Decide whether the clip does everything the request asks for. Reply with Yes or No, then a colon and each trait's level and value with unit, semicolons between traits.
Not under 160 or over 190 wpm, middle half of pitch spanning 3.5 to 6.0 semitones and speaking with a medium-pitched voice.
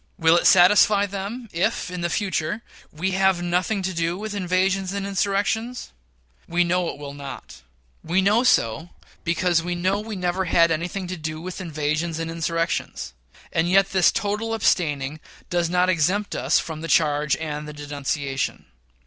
No: average, 165 wpm; average, 3.1 semitones; medium, 175 Hz